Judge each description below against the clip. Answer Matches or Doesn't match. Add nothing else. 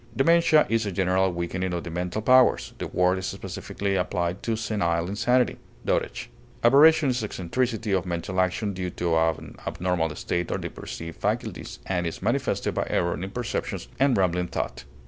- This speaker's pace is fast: Doesn't match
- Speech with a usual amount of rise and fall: Matches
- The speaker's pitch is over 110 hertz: Doesn't match